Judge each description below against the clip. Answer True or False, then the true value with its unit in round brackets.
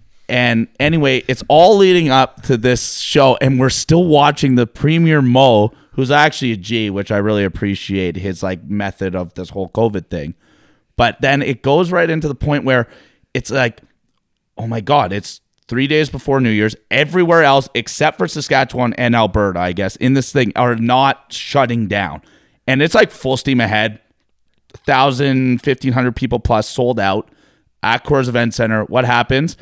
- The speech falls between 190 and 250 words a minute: False (175 wpm)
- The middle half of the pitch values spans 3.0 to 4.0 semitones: False (4.4 semitones)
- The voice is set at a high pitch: False (125 Hz)